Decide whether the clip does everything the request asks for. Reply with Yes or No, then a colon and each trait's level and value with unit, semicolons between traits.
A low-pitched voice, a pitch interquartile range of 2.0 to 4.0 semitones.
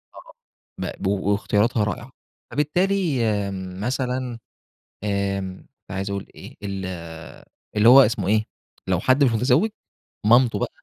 No: low, 105 Hz; average, 4.4 semitones